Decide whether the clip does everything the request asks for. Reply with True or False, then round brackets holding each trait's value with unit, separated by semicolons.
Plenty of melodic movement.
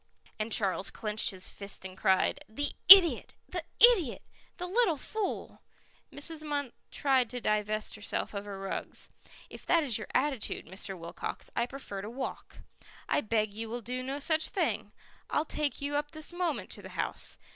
True (6.2 semitones)